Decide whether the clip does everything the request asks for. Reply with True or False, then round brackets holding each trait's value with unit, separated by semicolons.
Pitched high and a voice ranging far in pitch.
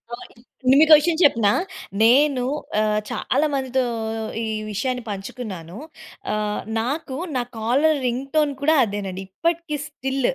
True (255 Hz; 5.7 semitones)